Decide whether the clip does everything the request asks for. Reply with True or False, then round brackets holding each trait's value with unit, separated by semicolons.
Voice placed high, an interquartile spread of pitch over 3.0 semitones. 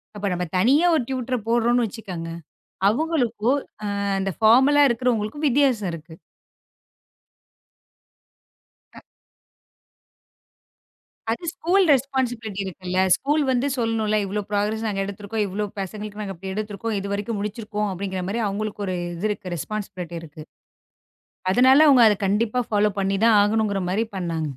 True (215 Hz; 3.6 semitones)